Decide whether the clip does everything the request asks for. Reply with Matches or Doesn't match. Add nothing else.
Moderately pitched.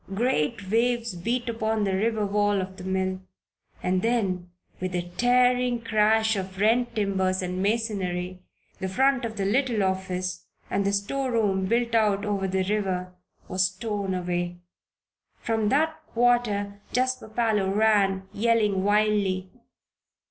Doesn't match